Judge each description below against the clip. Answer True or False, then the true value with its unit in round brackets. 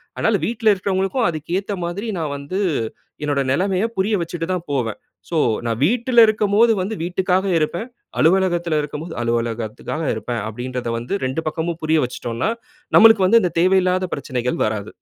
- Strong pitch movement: True (6.9 semitones)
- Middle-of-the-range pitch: True (170 Hz)